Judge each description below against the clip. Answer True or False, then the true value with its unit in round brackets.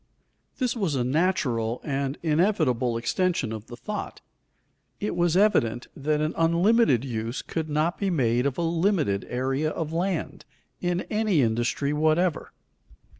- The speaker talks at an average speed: True (145 wpm)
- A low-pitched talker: False (155 Hz)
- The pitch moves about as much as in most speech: False (6.1 semitones)